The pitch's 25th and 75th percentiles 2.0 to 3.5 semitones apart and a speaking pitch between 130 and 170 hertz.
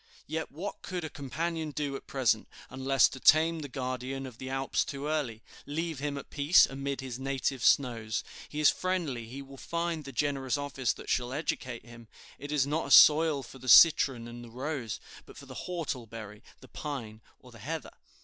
Yes: average, 3.2 semitones; low, 135 Hz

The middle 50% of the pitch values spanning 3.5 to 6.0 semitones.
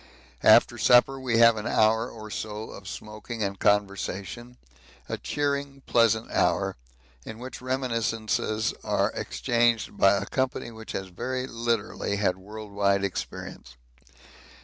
No: average, 2.9 semitones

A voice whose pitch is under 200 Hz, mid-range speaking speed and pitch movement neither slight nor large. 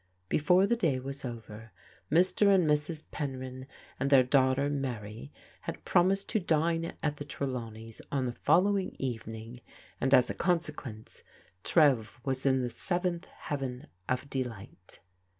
Yes: low, 135 Hz; average, 145 wpm; average, 4.8 semitones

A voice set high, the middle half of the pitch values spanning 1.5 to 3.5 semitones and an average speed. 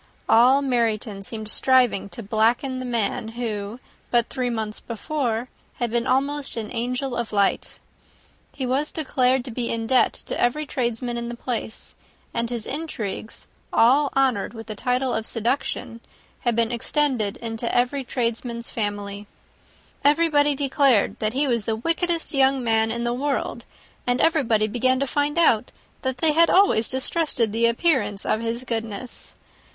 Yes: high, 240 Hz; average, 3.1 semitones; average, 155 wpm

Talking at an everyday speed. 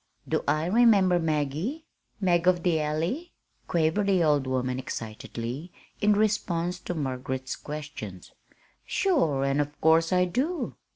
No: slow, 130 wpm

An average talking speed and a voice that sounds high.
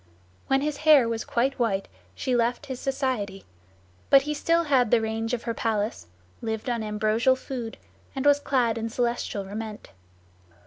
Yes: average, 165 wpm; high, 235 Hz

